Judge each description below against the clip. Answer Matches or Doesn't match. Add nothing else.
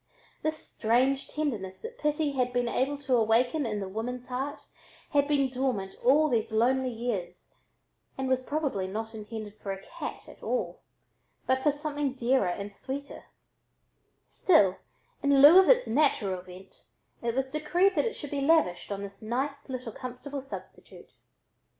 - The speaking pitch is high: Matches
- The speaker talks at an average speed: Matches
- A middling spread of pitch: Matches